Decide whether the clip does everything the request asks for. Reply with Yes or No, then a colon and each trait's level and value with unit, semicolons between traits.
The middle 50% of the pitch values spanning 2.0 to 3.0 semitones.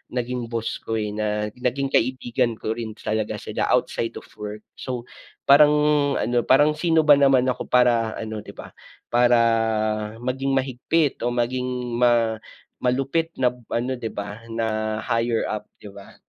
Yes: narrow, 2.6 semitones